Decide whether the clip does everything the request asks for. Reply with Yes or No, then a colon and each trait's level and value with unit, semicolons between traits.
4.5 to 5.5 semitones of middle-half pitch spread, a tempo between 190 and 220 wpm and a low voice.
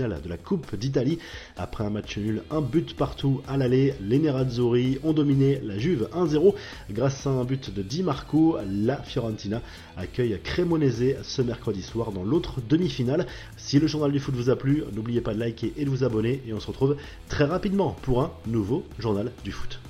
Yes: average, 5.0 semitones; average, 195 wpm; low, 130 Hz